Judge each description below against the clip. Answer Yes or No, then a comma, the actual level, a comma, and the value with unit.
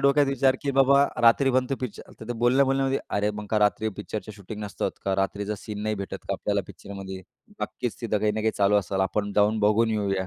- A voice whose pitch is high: No, low, 110 Hz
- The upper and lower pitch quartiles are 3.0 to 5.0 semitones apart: Yes, average, 4.3 semitones